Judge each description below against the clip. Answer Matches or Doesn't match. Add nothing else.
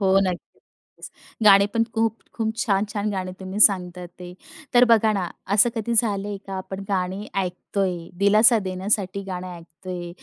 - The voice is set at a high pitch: Matches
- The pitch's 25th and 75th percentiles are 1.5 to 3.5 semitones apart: Matches